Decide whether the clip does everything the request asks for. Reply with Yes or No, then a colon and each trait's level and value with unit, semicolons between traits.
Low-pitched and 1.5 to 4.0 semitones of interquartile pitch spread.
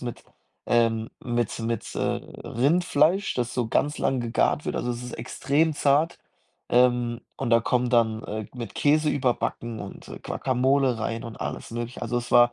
Yes: low, 120 Hz; narrow, 2.6 semitones